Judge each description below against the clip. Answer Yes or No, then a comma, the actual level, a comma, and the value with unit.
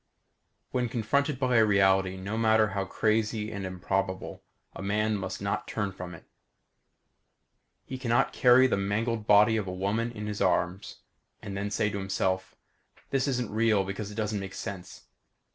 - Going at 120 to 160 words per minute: No, average, 170 wpm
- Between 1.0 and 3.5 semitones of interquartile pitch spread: Yes, narrow, 2.6 semitones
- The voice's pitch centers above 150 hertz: No, low, 105 Hz